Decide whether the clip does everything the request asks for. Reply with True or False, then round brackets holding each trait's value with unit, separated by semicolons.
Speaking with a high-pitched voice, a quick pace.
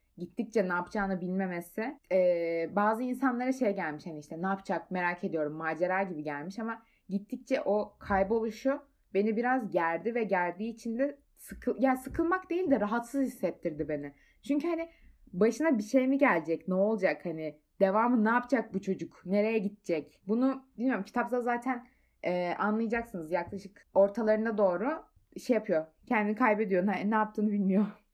True (210 Hz; 150 wpm)